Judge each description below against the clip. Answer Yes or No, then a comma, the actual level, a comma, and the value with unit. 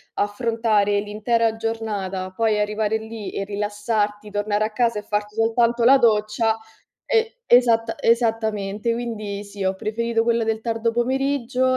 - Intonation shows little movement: Yes, narrow, 2.0 semitones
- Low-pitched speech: No, high, 220 Hz